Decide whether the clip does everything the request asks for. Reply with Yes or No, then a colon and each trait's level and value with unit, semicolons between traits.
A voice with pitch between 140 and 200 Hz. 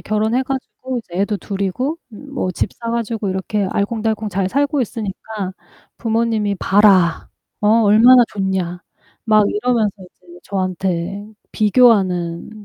No: high, 210 Hz